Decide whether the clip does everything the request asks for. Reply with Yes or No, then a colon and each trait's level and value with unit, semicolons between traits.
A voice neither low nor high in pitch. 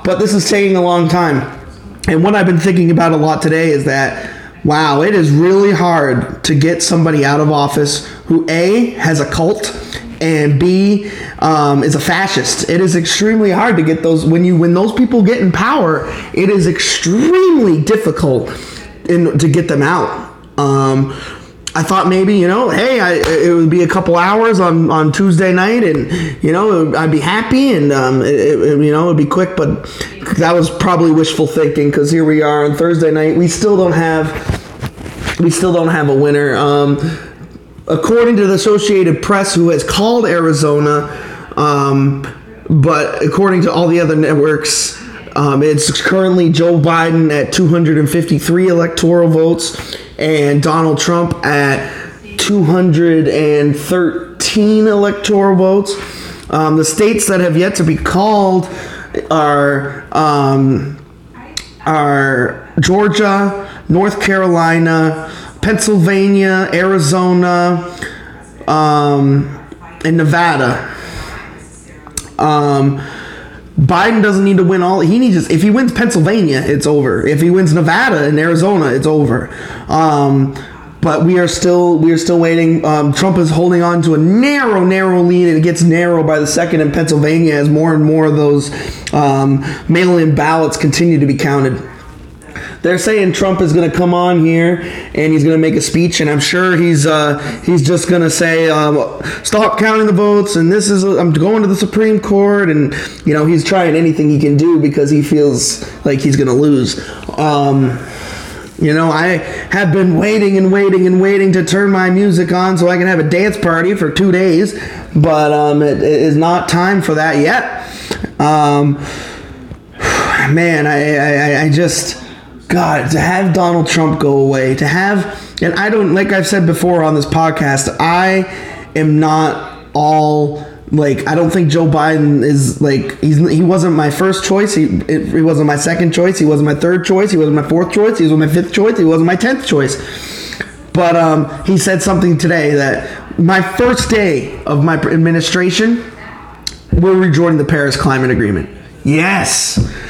Yes: medium, 165 Hz